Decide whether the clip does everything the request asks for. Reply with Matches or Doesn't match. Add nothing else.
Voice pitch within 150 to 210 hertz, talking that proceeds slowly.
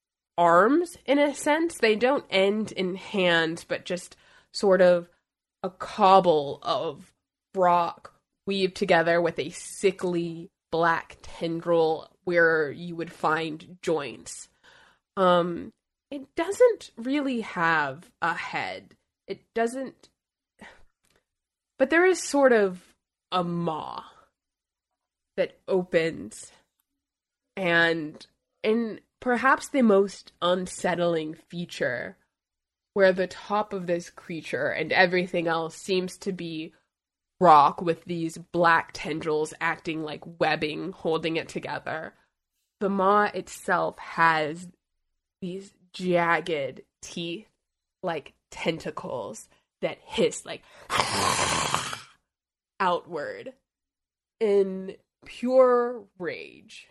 Matches